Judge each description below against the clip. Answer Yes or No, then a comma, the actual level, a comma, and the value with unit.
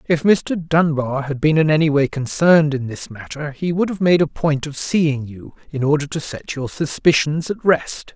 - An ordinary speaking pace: No, fast, 215 wpm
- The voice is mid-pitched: Yes, medium, 150 Hz